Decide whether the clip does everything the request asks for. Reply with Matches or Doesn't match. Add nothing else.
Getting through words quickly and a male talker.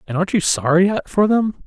Matches